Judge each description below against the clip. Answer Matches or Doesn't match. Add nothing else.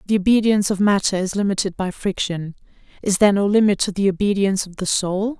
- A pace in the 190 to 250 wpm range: Matches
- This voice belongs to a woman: Matches